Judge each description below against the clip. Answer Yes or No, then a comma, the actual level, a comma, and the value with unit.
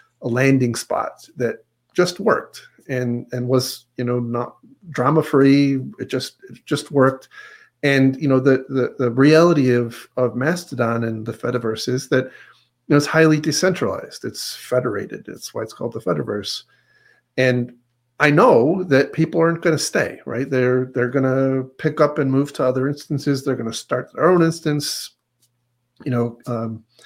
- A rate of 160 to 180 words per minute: Yes, average, 175 wpm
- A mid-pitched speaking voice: No, low, 130 Hz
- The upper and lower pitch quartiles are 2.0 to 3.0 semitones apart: No, average, 3.5 semitones